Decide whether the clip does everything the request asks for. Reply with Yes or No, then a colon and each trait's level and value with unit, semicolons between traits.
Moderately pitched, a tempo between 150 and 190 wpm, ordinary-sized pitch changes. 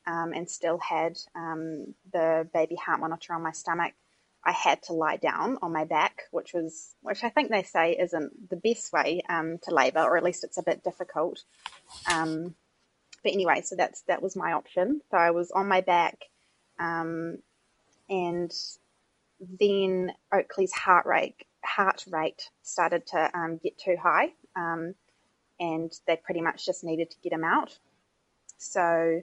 No: medium, 170 Hz; average, 170 wpm; narrow, 2.0 semitones